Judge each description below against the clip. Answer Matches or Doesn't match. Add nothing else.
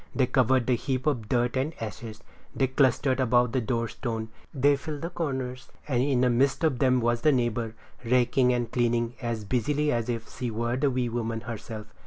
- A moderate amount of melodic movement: Doesn't match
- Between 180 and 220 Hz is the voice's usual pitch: Doesn't match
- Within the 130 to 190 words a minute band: Doesn't match